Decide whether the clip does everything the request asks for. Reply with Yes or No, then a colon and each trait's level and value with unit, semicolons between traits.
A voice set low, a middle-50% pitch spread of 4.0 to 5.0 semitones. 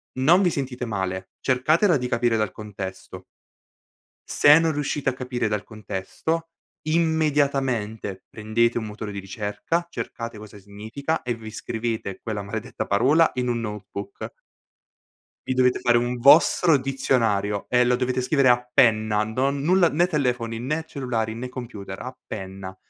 Yes: low, 120 Hz; average, 4.5 semitones